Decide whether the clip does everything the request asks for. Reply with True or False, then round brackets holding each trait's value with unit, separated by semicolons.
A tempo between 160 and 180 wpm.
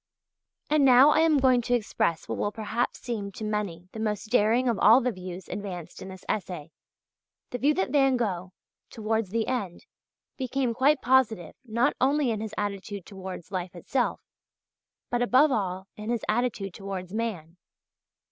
True (165 wpm)